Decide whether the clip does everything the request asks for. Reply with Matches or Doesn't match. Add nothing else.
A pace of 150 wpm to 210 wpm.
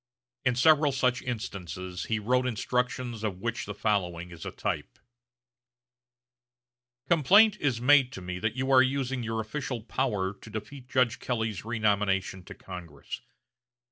Doesn't match